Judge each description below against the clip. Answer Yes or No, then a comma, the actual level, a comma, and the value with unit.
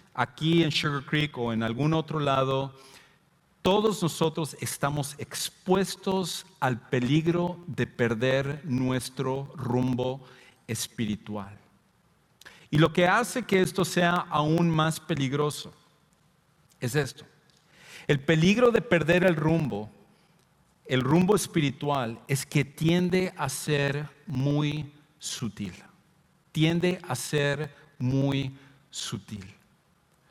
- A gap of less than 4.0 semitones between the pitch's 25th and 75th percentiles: No, average, 4.3 semitones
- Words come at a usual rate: No, slow, 105 wpm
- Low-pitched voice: No, medium, 150 Hz